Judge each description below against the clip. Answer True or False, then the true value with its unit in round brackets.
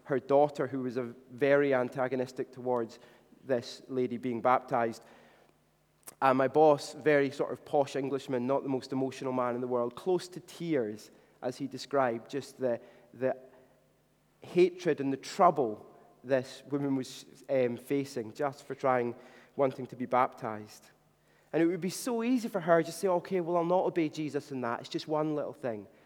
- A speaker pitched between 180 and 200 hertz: False (135 Hz)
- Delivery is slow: False (180 wpm)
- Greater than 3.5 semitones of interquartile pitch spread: False (3.1 semitones)